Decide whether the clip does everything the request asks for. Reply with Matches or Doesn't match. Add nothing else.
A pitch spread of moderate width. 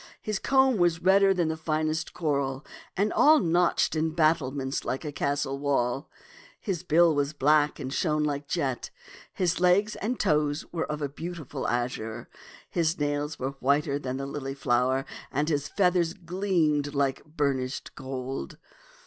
Matches